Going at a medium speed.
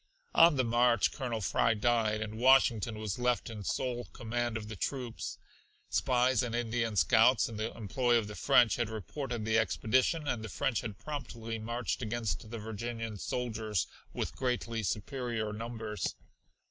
Yes: average, 160 wpm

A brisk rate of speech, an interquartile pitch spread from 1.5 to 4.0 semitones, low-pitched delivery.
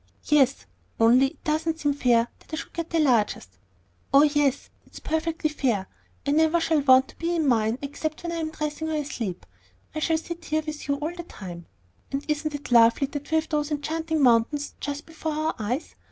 No: fast, 210 wpm; average, 3.4 semitones; very high, 295 Hz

